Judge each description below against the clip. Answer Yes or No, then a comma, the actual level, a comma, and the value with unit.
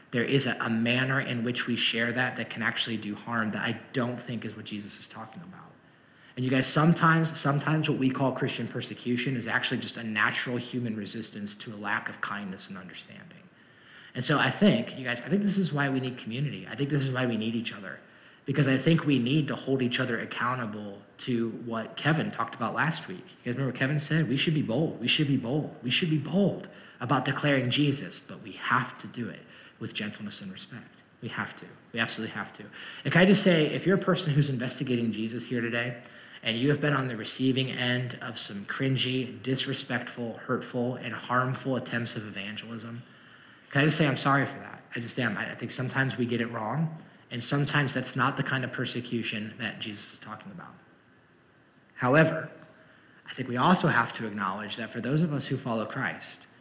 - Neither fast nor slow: No, fast, 215 wpm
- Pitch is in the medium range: No, low, 130 Hz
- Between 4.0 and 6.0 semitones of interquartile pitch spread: No, average, 3.4 semitones